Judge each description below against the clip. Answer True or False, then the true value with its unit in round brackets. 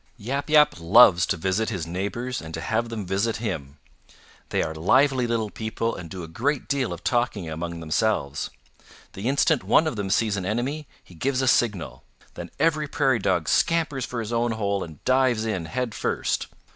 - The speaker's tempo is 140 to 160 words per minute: False (190 wpm)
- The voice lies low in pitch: True (110 Hz)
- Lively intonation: True (5.7 semitones)